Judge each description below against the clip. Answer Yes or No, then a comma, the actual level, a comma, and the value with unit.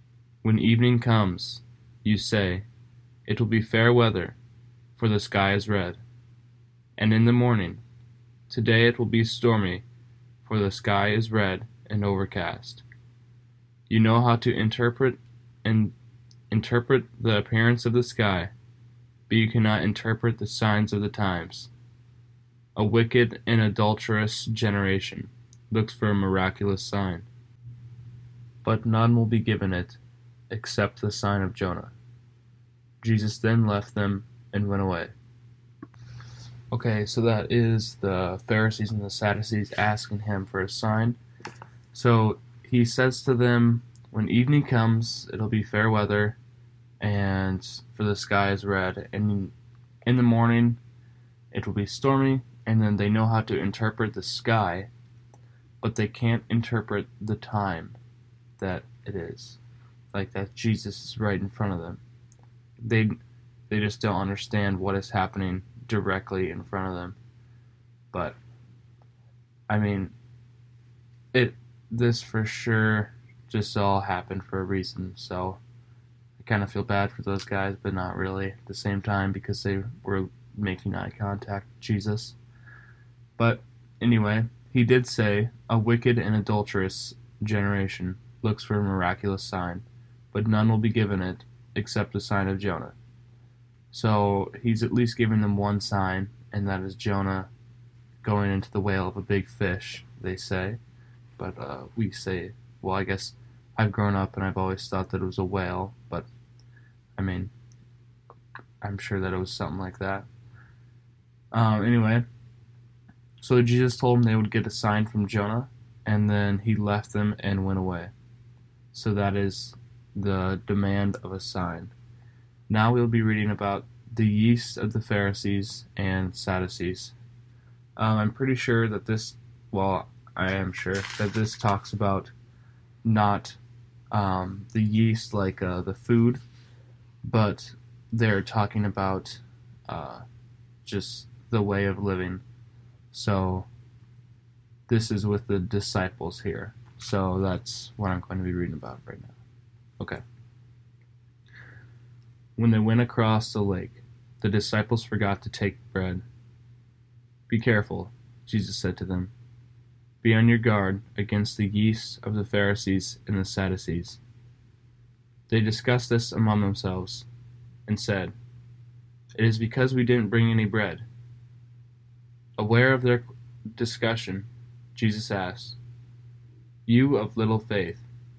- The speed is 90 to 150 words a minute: Yes, average, 140 wpm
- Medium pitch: No, low, 115 Hz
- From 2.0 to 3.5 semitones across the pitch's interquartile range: Yes, average, 2.9 semitones